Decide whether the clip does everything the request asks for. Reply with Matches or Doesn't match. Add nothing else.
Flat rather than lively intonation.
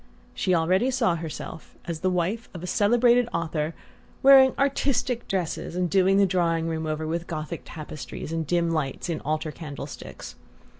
Doesn't match